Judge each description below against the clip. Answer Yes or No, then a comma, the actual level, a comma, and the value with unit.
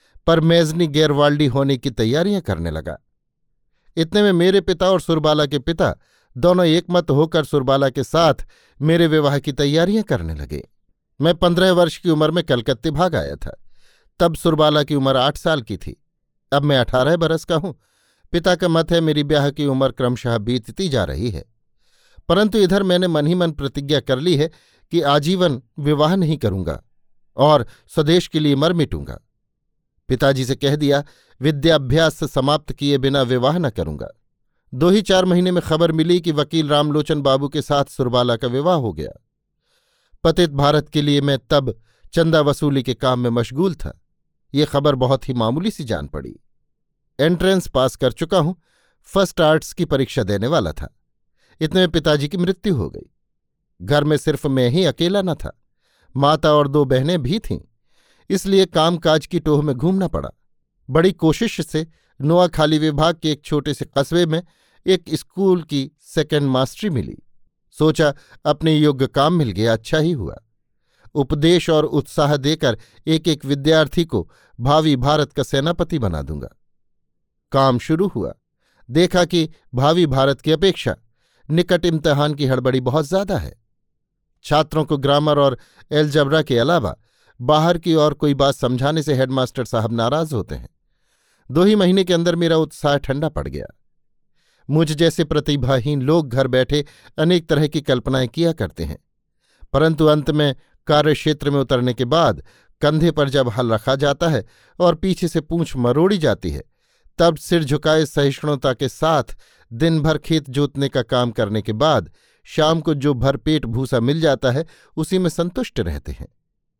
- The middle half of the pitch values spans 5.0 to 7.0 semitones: No, average, 3.7 semitones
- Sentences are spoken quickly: No, average, 165 wpm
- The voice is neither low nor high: Yes, medium, 150 Hz